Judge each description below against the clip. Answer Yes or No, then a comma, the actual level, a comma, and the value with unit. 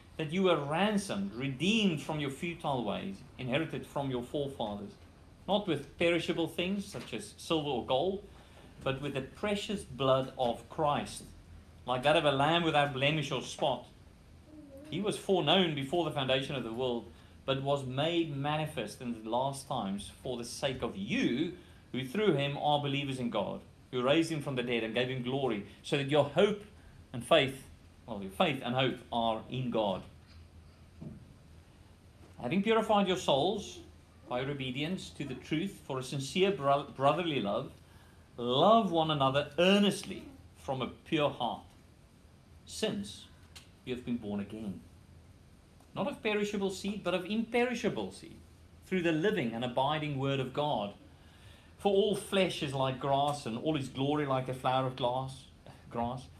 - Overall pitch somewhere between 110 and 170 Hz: Yes, low, 135 Hz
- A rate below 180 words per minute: Yes, average, 165 wpm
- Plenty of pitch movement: Yes, wide, 6.5 semitones